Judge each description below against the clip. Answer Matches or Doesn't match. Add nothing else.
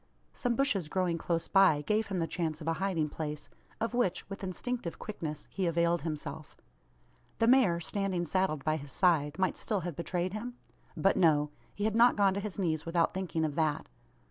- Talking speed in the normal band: Matches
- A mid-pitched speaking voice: Matches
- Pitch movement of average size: Matches